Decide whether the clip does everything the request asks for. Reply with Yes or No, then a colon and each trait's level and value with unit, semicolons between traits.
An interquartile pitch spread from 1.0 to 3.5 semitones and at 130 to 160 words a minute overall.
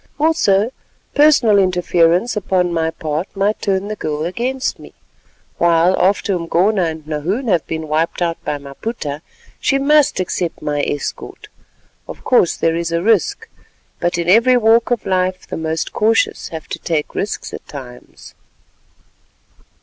No: average, 5.0 semitones; average, 150 wpm